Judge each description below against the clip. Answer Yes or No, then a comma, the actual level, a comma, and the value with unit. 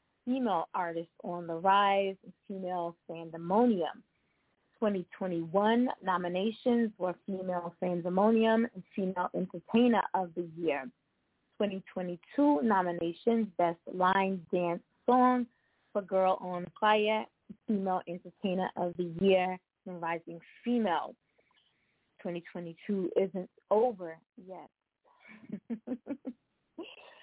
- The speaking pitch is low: No, high, 190 Hz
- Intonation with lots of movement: No, average, 4.1 semitones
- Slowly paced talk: Yes, slow, 85 wpm